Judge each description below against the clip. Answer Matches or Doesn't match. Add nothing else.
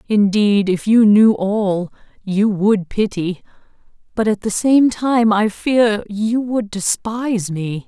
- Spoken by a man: Doesn't match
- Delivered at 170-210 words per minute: Doesn't match